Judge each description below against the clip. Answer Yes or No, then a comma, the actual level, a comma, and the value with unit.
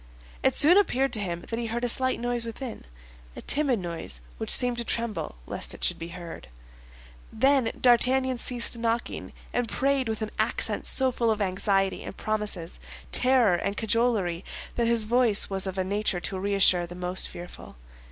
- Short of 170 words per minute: No, average, 175 wpm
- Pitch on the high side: Yes, high, 220 Hz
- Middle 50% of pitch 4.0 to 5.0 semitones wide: Yes, average, 4.7 semitones